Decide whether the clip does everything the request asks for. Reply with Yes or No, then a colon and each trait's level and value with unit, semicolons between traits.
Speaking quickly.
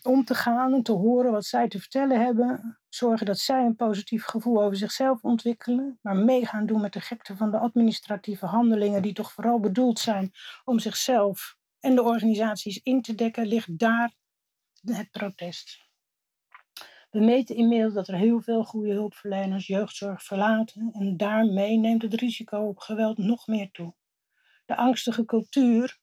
No: average, 165 wpm